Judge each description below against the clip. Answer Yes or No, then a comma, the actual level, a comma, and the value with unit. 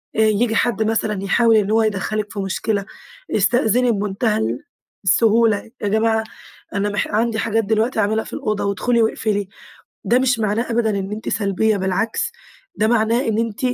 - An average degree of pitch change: No, narrow, 1.9 semitones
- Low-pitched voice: No, high, 220 Hz